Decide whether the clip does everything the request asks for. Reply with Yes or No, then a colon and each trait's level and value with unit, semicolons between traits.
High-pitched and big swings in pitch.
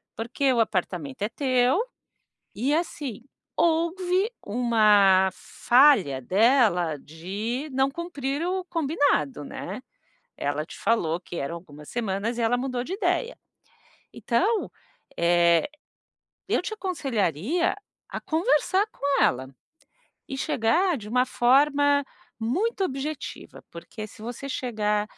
Yes: high, 245 Hz; wide, 7.5 semitones